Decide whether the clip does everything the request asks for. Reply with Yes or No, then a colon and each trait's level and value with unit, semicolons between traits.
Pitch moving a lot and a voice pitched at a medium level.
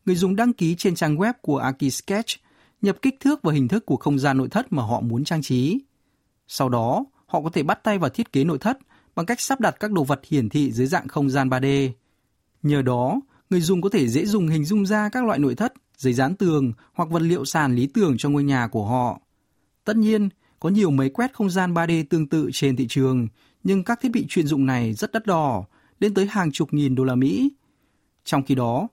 Yes: wide, 7.2 semitones; medium, 160 Hz